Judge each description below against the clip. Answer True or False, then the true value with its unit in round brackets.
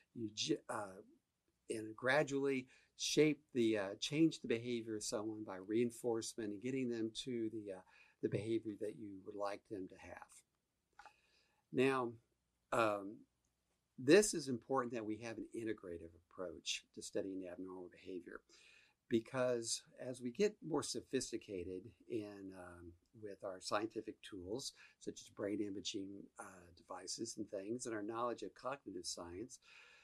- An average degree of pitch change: True (3.8 semitones)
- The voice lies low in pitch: True (110 Hz)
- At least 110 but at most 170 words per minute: True (140 wpm)